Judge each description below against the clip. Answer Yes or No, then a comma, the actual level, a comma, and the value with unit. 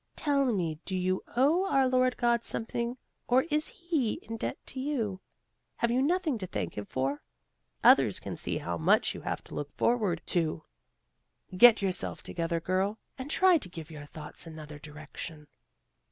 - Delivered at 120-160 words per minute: No, average, 170 wpm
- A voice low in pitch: No, high, 205 Hz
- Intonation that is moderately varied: No, wide, 8.4 semitones